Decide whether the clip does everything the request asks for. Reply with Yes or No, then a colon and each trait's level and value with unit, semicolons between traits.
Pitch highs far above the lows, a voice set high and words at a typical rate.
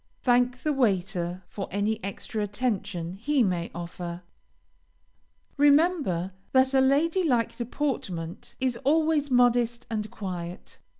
No: wide, 6.5 semitones; high, 235 Hz; slow, 115 wpm